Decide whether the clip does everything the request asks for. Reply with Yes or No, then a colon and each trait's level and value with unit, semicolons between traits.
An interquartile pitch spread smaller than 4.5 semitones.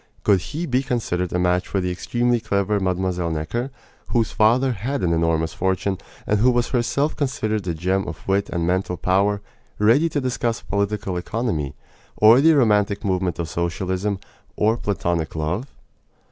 No: average, 4.9 semitones